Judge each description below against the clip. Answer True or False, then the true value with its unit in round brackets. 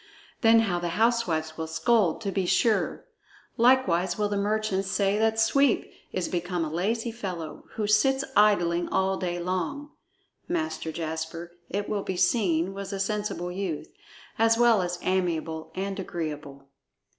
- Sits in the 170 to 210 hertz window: True (190 Hz)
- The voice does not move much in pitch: False (4.1 semitones)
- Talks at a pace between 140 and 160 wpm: True (150 wpm)